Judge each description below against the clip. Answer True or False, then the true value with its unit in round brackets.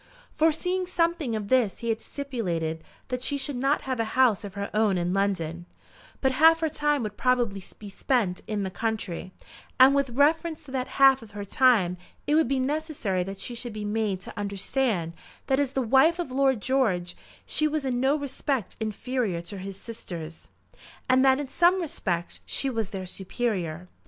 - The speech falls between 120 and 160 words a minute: False (185 wpm)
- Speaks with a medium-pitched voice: False (240 Hz)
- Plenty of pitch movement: True (5.7 semitones)